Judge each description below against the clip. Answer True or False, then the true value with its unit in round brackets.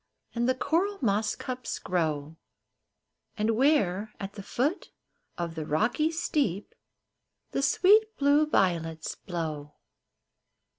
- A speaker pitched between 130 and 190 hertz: False (215 Hz)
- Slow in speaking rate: True (110 wpm)